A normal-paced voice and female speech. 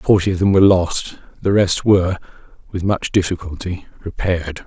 No: average, 155 wpm; male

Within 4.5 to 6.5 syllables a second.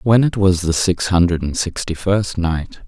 No: 4.3 syllables/s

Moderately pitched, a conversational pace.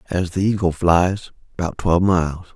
No: very low, 90 Hz; average, 165 wpm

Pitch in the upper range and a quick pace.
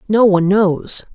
No: high, 195 Hz; average, 160 wpm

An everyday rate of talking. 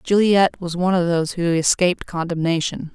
Yes: average, 165 wpm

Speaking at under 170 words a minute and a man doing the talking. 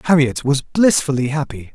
Yes: average, 140 wpm; male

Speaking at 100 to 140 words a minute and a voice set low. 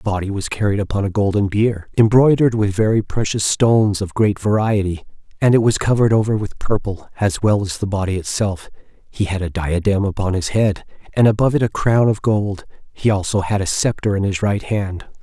No: fast, 205 wpm; low, 100 Hz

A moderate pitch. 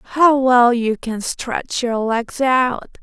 No: high, 245 Hz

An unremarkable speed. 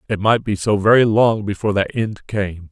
No: fast, 220 wpm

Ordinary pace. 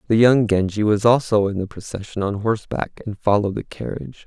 Yes: average, 195 wpm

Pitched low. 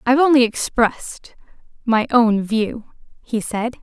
No: high, 235 Hz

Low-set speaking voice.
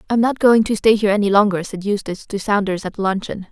No: high, 205 Hz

